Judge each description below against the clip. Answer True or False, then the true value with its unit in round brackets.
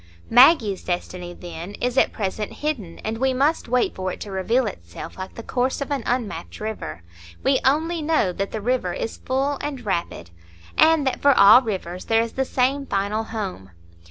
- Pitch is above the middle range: True (225 Hz)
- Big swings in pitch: True (5.8 semitones)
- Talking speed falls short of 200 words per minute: True (185 wpm)